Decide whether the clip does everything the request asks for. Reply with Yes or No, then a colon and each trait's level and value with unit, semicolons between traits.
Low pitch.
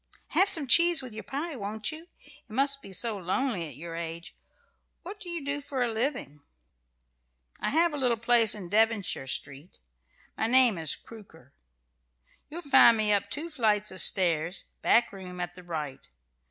No: high, 220 Hz